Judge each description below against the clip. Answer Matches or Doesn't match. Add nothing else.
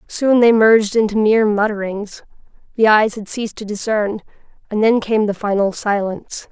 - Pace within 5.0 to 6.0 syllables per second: Matches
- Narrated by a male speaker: Doesn't match